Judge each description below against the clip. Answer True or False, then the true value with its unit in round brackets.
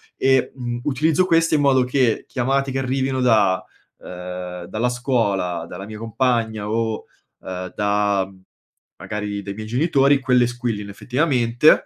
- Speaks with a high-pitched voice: False (120 Hz)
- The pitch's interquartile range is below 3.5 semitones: False (4.2 semitones)